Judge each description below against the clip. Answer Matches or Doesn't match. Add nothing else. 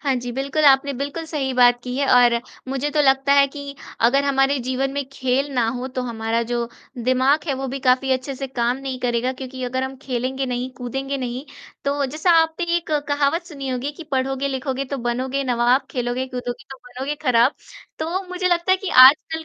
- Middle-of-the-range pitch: Doesn't match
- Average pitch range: Doesn't match